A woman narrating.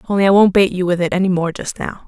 Yes: female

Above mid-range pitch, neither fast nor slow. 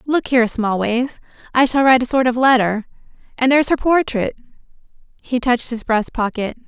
Yes: high, 245 Hz; average, 160 wpm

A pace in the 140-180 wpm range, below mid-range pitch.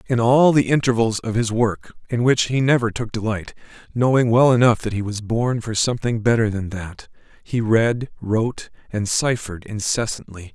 Yes: average, 165 wpm; low, 115 Hz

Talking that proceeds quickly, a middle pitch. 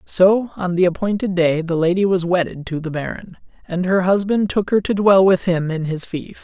Yes: fast, 225 wpm; medium, 180 Hz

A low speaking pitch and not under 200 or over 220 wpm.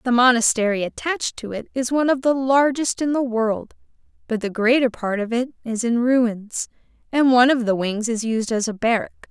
No: high, 240 Hz; fast, 205 wpm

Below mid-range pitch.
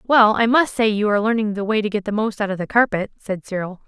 No: high, 210 Hz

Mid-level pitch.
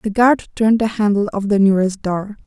No: high, 210 Hz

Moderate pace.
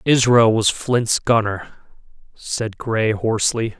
No: slow, 110 wpm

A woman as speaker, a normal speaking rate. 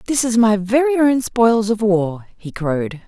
Yes: female; average, 195 wpm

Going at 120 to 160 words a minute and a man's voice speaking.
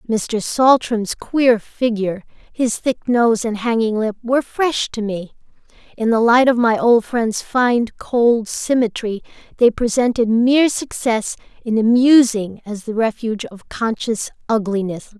No: average, 140 wpm; female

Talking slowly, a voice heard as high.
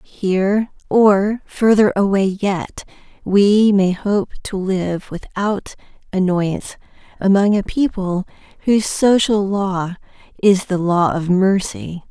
Yes: slow, 115 wpm; high, 195 Hz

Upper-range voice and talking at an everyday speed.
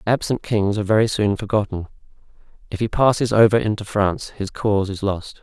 No: low, 105 Hz; average, 175 wpm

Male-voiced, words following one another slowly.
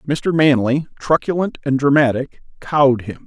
Yes: male; slow, 130 wpm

